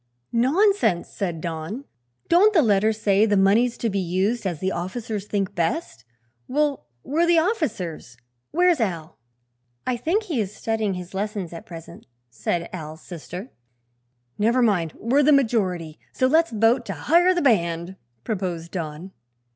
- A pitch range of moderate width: No, wide, 7.0 semitones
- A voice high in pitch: Yes, high, 210 Hz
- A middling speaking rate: Yes, average, 155 wpm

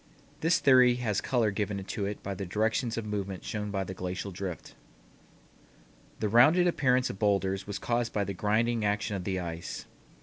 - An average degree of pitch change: Yes, average, 3.3 semitones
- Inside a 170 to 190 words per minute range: Yes, average, 180 wpm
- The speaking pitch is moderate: No, low, 105 Hz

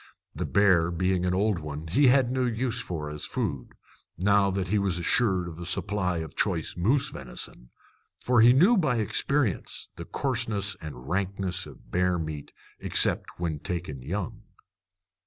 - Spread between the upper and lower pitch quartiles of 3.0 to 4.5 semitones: No, average, 4.9 semitones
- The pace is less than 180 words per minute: Yes, average, 165 wpm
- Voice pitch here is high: No, very low, 95 Hz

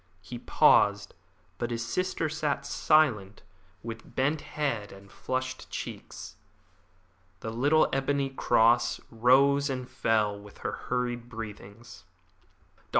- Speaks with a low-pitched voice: Yes, low, 120 Hz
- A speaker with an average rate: No, slow, 115 wpm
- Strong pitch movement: No, average, 3.8 semitones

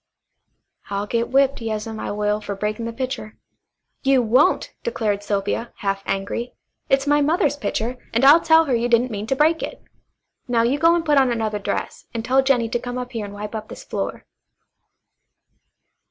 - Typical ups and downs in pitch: Yes, average, 4.2 semitones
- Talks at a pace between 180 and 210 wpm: Yes, average, 185 wpm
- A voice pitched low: No, high, 235 Hz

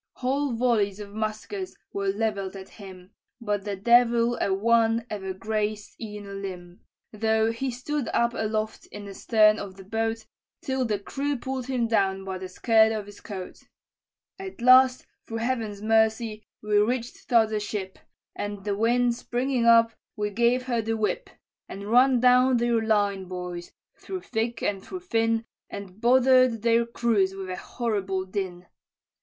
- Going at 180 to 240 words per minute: No, average, 160 wpm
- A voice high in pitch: Yes, high, 220 Hz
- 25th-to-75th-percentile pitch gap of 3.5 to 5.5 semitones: No, average, 3.0 semitones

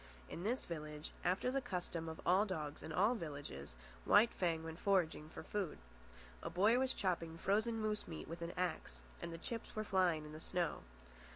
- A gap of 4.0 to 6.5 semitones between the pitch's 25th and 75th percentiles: Yes, average, 4.3 semitones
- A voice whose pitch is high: No, medium, 175 Hz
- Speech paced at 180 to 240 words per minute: Yes, average, 190 wpm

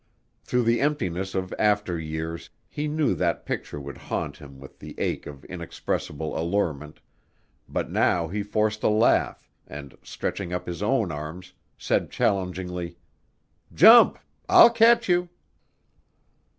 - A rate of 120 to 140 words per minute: Yes, slow, 135 wpm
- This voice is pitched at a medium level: No, very low, 90 Hz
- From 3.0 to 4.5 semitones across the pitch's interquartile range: No, average, 5.2 semitones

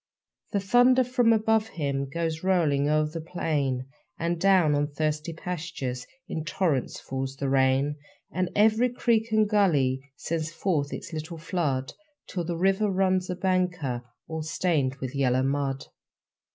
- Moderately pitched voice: Yes, medium, 165 Hz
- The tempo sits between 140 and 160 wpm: Yes, average, 150 wpm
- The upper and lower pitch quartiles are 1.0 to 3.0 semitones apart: No, average, 5.1 semitones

